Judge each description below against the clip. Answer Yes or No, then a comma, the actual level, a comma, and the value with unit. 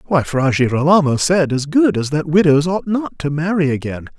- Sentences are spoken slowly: No, average, 200 wpm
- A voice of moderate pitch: Yes, medium, 155 Hz